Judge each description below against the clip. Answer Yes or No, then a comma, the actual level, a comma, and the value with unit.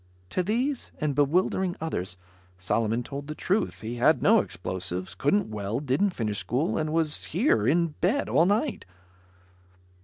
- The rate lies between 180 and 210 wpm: No, average, 150 wpm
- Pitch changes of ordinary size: No, wide, 8.8 semitones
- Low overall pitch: No, medium, 150 Hz